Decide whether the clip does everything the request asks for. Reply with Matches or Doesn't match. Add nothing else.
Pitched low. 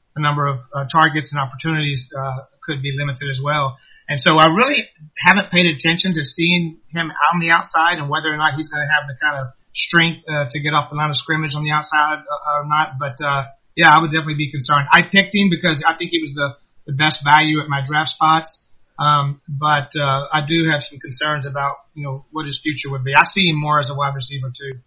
Doesn't match